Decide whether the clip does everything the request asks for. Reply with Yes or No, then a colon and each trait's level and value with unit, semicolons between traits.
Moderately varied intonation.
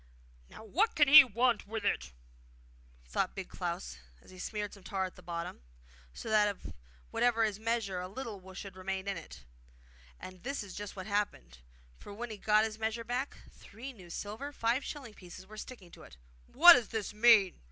Yes: average, 3.8 semitones